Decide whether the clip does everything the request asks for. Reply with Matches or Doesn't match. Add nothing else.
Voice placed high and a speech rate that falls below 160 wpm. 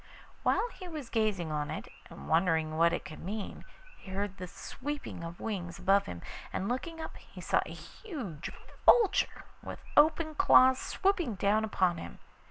Doesn't match